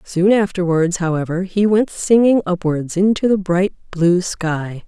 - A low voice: No, medium, 185 Hz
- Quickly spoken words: No, average, 150 wpm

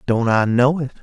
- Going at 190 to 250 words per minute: Yes, fast, 235 wpm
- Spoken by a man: Yes, male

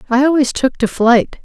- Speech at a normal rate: No, fast, 210 wpm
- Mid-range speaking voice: No, very high, 255 Hz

